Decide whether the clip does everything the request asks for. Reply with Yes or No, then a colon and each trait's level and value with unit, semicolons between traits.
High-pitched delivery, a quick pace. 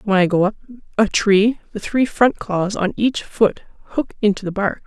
Yes: high, 210 Hz; fast, 210 wpm